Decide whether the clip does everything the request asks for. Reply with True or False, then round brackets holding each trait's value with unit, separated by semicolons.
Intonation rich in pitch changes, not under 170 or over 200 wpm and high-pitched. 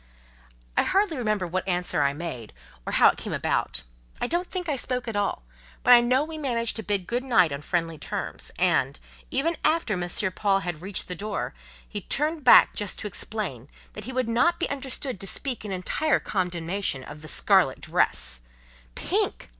True (6.8 semitones; 190 wpm; 210 Hz)